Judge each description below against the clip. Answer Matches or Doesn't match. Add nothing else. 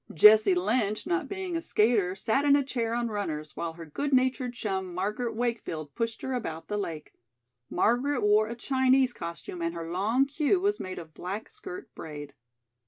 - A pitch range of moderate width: Doesn't match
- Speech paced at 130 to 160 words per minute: Doesn't match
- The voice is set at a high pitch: Matches